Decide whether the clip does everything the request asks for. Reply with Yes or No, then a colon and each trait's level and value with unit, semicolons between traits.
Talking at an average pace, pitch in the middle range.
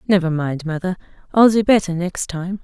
Yes: average, 180 wpm; medium, 180 Hz